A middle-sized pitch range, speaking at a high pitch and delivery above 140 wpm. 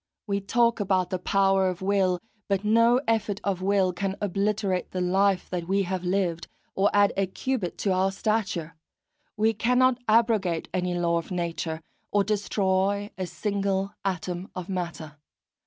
No: narrow, 2.1 semitones; high, 195 Hz; average, 160 wpm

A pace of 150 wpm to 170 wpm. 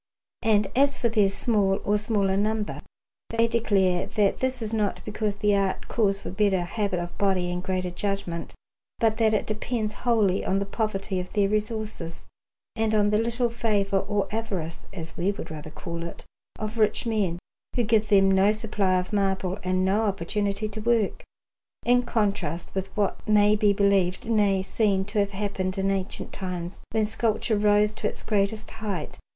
No: average, 180 wpm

